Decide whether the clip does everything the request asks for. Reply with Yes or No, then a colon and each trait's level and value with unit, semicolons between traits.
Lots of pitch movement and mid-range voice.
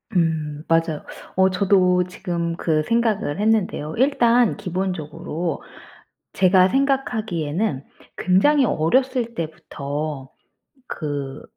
Yes: wide, 5.8 semitones; medium, 180 Hz